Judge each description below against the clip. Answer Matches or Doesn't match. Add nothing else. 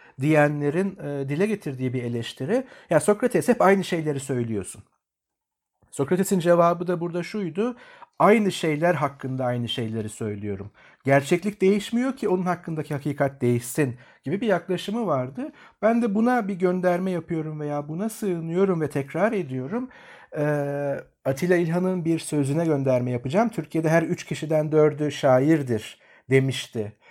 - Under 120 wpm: Doesn't match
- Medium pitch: Matches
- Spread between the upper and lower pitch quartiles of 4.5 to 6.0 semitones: Matches